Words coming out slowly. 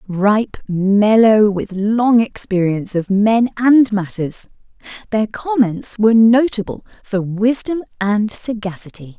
Yes: slow, 110 wpm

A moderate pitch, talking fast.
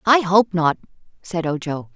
No: medium, 180 Hz; average, 155 wpm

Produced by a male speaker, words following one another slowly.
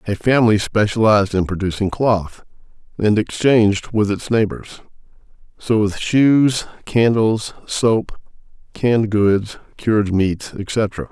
Yes: male; slow, 115 wpm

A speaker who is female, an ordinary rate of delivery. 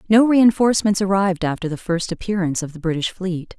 Yes: female; average, 185 wpm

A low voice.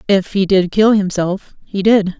No: high, 195 Hz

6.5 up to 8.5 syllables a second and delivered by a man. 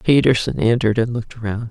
No: 6.8 syllables/s; female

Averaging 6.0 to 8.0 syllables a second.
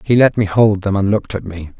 Yes: 6.1 syllables/s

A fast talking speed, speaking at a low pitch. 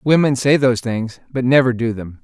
Yes: fast, 215 wpm; low, 125 Hz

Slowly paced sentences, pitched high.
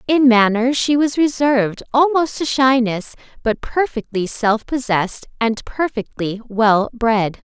Yes: slow, 130 wpm; high, 240 Hz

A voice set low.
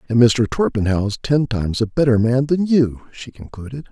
Yes: low, 120 Hz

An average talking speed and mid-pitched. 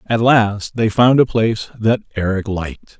No: average, 180 wpm; low, 110 Hz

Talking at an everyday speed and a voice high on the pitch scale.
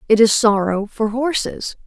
Yes: average, 160 wpm; high, 225 Hz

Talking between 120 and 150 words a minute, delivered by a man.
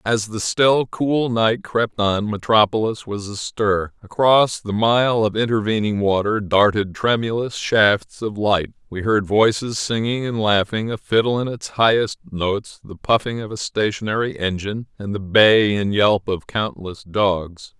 No: average, 160 wpm; male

